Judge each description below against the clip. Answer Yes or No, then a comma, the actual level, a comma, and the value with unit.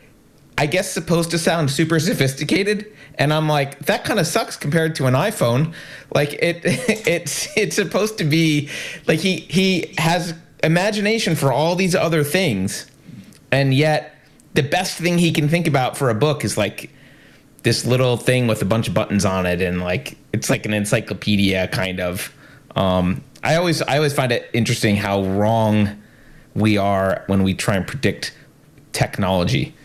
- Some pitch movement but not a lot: No, wide, 6.8 semitones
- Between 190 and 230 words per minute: No, average, 170 wpm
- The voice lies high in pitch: No, medium, 145 Hz